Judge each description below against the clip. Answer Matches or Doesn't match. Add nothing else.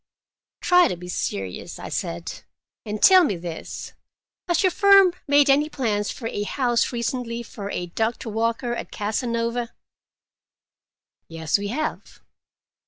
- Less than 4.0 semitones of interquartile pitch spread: Doesn't match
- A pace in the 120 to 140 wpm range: Matches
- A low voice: Doesn't match